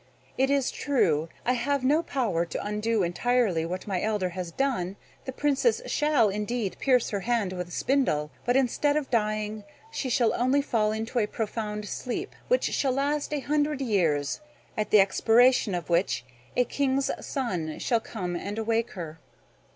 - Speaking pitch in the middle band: No, high, 225 Hz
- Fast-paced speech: No, average, 170 wpm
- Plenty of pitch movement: Yes, wide, 5.7 semitones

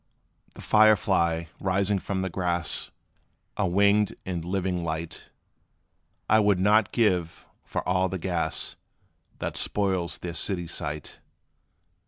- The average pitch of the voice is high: No, very low, 95 Hz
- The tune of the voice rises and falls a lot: No, average, 2.8 semitones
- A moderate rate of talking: No, slow, 125 wpm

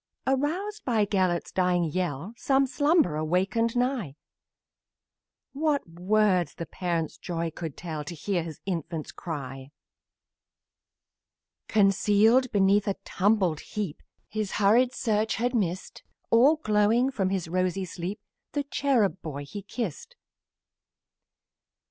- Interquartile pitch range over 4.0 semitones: Yes, wide, 5.4 semitones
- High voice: Yes, high, 195 Hz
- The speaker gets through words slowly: Yes, slow, 115 wpm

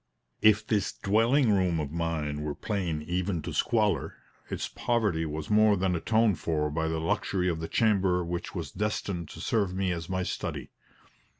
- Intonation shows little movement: No, average, 4.3 semitones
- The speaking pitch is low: Yes, very low, 90 Hz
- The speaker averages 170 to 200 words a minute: Yes, average, 175 wpm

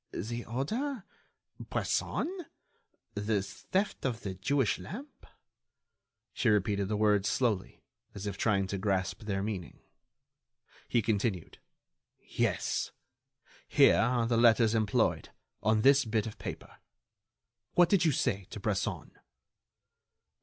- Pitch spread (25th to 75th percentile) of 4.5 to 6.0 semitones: No, average, 4.0 semitones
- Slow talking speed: Yes, slow, 115 wpm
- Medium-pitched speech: No, low, 110 Hz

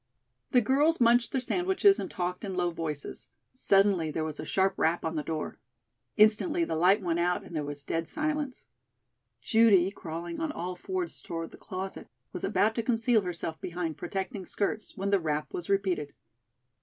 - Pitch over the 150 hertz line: Yes, high, 190 Hz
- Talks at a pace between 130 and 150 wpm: No, average, 180 wpm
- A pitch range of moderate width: No, wide, 5.7 semitones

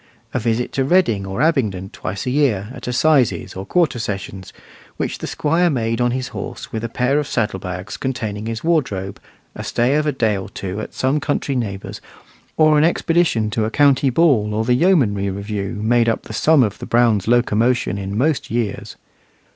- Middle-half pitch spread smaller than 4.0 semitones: No, average, 5.3 semitones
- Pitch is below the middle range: Yes, low, 120 Hz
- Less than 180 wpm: No, average, 195 wpm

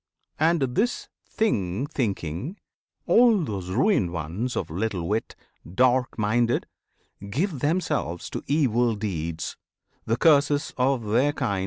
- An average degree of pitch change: No, wide, 7.0 semitones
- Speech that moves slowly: Yes, slow, 120 wpm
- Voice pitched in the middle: No, low, 120 Hz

